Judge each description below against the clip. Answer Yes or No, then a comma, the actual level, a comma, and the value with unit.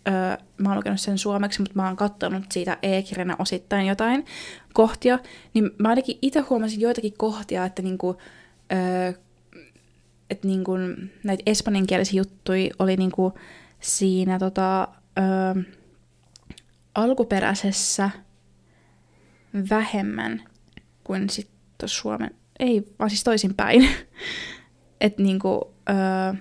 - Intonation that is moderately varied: No, narrow, 2.1 semitones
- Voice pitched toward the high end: Yes, high, 195 Hz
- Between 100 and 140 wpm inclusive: Yes, average, 105 wpm